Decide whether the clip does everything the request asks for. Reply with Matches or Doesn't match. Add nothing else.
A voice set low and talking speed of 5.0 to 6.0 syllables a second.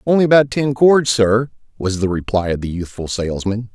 Matches